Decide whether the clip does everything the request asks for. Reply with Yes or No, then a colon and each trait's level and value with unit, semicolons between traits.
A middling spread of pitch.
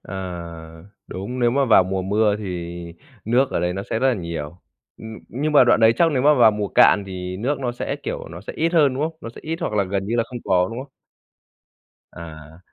No: wide, 5.7 semitones